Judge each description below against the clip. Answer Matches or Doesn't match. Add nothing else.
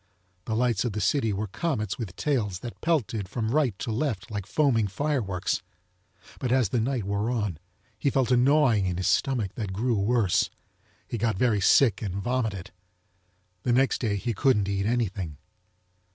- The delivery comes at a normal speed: Matches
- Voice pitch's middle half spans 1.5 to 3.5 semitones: Doesn't match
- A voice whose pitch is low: Matches